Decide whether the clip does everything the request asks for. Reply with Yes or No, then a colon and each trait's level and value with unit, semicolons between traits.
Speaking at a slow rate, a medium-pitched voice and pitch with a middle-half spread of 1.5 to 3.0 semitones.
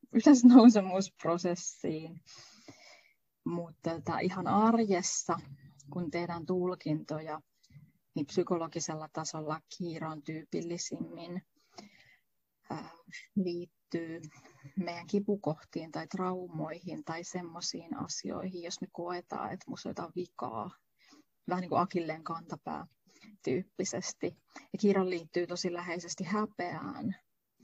Yes: slow, 85 wpm; medium, 175 Hz; narrow, 2.6 semitones